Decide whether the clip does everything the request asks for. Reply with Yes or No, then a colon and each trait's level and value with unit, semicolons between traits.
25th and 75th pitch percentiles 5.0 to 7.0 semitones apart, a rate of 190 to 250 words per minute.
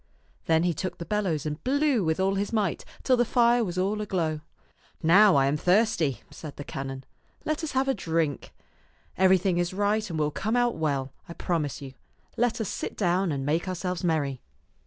Yes: average, 5.3 semitones; average, 200 wpm